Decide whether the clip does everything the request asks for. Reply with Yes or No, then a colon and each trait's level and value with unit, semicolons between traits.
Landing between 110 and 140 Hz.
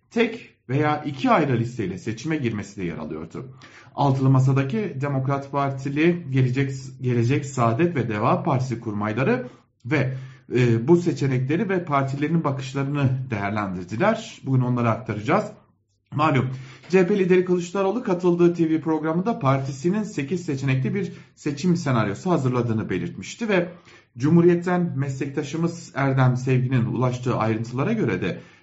Yes: low, 135 Hz